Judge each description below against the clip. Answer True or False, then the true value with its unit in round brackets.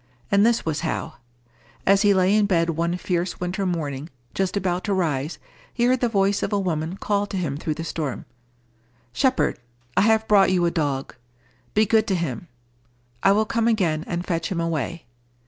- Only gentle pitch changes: False (3.6 semitones)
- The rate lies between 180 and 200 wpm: True (190 wpm)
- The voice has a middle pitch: True (180 Hz)